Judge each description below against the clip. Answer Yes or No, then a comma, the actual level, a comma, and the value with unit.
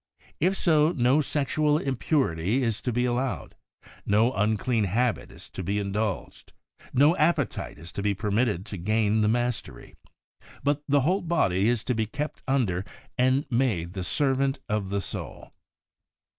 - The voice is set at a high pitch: No, low, 120 Hz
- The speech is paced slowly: No, average, 160 wpm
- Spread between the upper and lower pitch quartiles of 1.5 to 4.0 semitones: No, average, 5.2 semitones